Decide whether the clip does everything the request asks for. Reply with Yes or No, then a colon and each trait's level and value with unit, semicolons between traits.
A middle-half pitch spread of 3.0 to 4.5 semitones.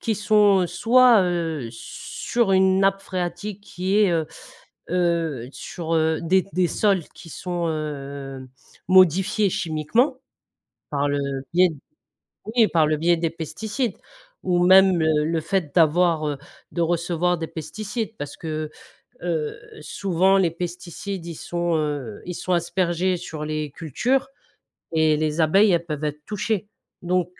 Yes: average, 3.4 semitones